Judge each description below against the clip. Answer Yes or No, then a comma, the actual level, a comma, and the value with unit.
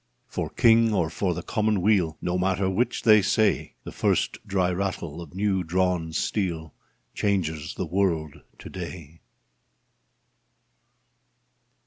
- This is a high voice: No, very low, 90 Hz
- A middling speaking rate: No, slow, 120 wpm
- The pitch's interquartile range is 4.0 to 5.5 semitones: No, average, 3.3 semitones